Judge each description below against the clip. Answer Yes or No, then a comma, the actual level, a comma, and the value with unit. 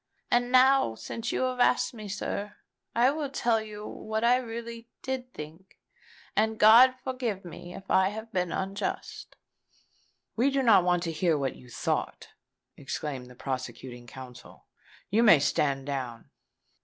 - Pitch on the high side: Yes, high, 210 Hz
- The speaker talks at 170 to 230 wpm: No, average, 155 wpm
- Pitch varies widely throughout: Yes, wide, 8.0 semitones